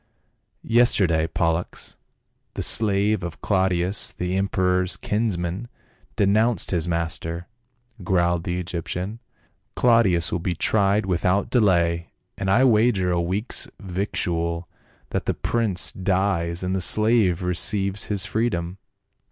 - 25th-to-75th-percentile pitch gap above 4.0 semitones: No, average, 3.1 semitones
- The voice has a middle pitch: No, very low, 95 Hz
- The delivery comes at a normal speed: No, slow, 125 wpm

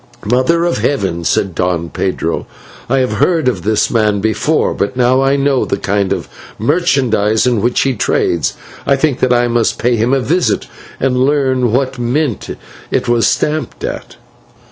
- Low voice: Yes, low, 125 Hz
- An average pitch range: Yes, average, 4.1 semitones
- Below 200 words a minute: Yes, average, 170 wpm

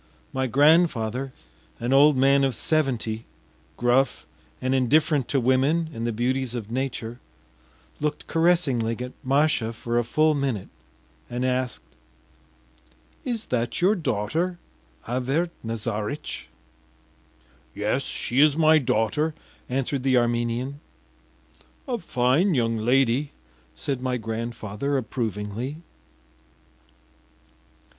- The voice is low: Yes, low, 125 Hz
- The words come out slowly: Yes, slow, 105 wpm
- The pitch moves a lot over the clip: No, average, 3.7 semitones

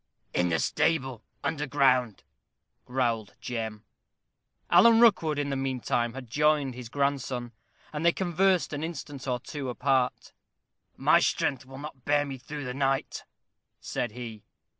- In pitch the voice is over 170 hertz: No, low, 135 Hz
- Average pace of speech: Yes, average, 145 wpm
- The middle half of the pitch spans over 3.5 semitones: No, average, 3.2 semitones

